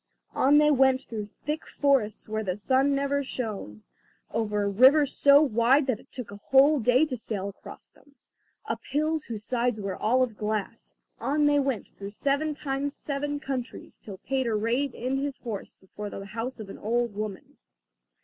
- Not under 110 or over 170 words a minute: No, average, 180 wpm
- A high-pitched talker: Yes, very high, 255 Hz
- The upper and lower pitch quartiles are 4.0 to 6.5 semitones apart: Yes, average, 4.8 semitones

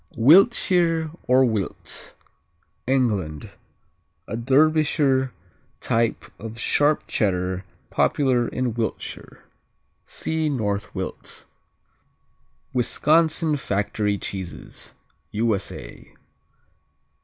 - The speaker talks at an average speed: No, slow, 70 wpm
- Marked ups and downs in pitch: Yes, wide, 6.4 semitones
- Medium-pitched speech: No, low, 125 Hz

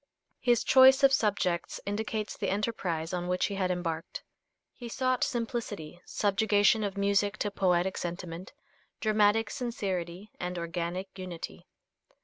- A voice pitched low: No, high, 200 Hz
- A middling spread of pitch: Yes, average, 3.6 semitones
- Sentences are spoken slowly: Yes, slow, 125 wpm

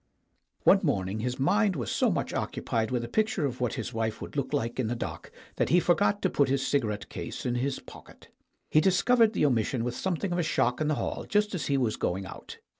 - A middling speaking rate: No, fast, 235 wpm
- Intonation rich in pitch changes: Yes, wide, 7.0 semitones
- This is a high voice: No, low, 135 Hz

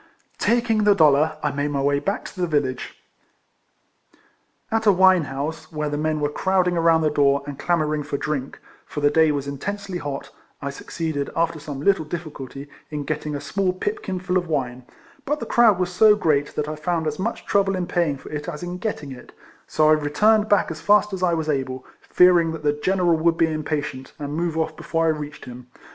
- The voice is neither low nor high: Yes, medium, 155 Hz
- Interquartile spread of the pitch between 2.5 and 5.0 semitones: Yes, average, 3.8 semitones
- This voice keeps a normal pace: No, fast, 210 wpm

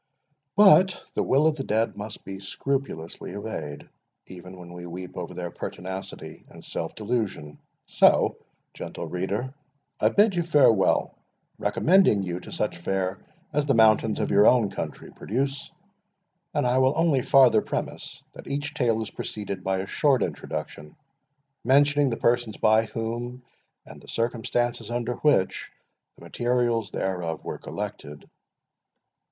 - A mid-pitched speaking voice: No, low, 115 Hz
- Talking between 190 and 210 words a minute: No, average, 145 wpm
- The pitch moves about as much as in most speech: No, wide, 5.7 semitones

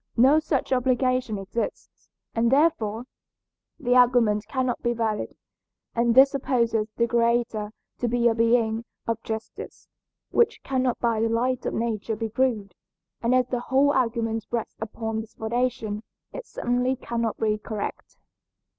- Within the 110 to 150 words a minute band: Yes, average, 145 wpm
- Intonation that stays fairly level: Yes, narrow, 2.2 semitones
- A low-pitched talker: No, high, 235 Hz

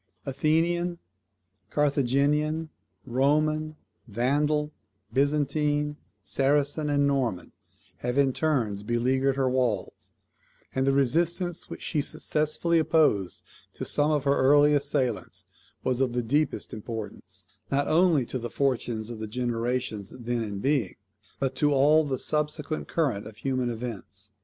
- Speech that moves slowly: Yes, slow, 130 wpm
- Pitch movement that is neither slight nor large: Yes, average, 3.7 semitones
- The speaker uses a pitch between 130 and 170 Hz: Yes, low, 135 Hz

